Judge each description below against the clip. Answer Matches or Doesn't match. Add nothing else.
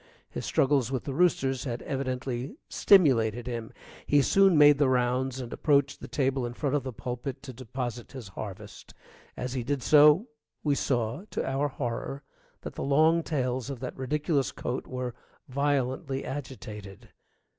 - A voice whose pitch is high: Doesn't match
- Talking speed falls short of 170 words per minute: Matches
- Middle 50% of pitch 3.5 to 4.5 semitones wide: Doesn't match